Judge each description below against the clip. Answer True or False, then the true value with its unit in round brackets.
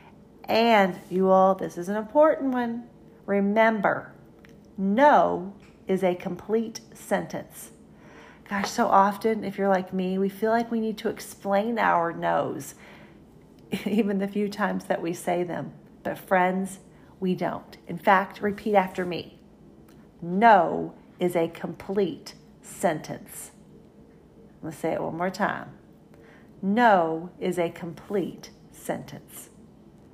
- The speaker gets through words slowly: True (125 wpm)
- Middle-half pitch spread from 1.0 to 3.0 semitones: True (2.6 semitones)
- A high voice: True (195 Hz)